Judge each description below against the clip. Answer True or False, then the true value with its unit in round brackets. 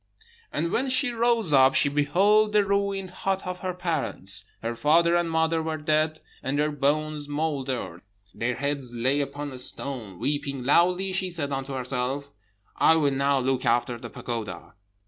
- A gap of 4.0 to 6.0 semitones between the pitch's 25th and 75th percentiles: True (4.5 semitones)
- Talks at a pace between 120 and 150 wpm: False (165 wpm)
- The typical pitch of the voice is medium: True (145 Hz)